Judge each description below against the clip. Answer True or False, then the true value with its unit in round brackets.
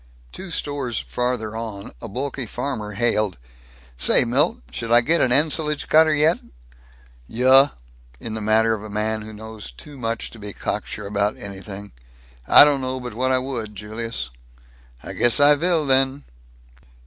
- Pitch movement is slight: False (4.2 semitones)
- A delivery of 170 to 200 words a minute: False (160 wpm)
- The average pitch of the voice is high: False (120 Hz)